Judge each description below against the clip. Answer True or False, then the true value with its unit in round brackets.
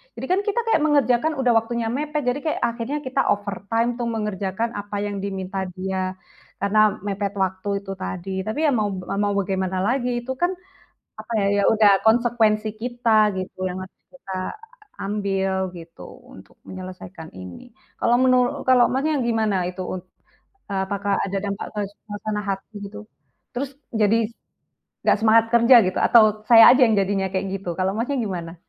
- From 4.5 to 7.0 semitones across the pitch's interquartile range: False (3.7 semitones)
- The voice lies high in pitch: True (210 Hz)